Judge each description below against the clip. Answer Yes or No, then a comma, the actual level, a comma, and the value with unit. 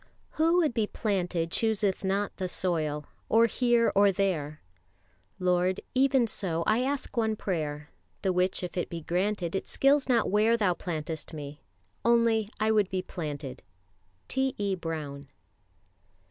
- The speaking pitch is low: No, high, 190 Hz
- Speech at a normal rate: Yes, average, 145 wpm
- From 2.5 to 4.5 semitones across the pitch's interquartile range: No, average, 5.1 semitones